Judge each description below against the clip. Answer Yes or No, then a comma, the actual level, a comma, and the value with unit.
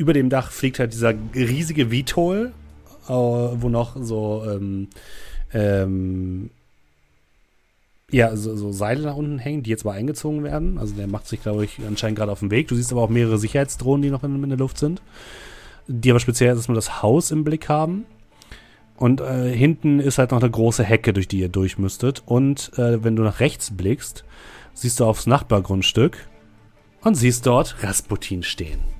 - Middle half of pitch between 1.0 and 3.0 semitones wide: No, average, 4.3 semitones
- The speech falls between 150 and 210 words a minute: Yes, average, 180 wpm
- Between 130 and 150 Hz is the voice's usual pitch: No, low, 120 Hz